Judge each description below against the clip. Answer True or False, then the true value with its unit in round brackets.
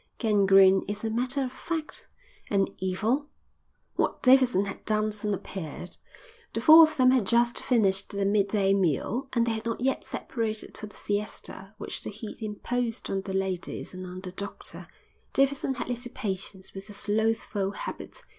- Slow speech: False (170 wpm)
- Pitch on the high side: True (215 Hz)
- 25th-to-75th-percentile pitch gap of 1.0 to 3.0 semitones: False (3.9 semitones)